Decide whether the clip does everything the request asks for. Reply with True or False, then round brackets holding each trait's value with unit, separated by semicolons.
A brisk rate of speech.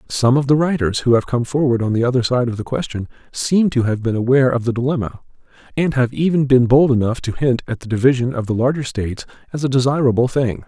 True (235 wpm)